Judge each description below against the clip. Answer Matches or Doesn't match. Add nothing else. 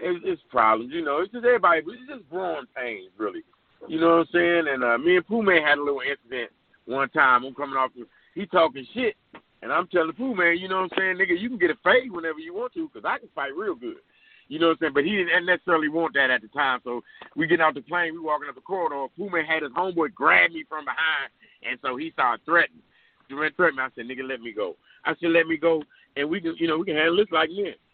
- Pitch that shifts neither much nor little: Doesn't match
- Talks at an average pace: Doesn't match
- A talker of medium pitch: Matches